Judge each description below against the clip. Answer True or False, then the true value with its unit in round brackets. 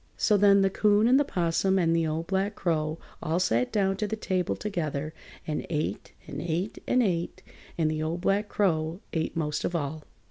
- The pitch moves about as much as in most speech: True (4.0 semitones)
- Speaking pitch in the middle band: True (175 Hz)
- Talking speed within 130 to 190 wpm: False (200 wpm)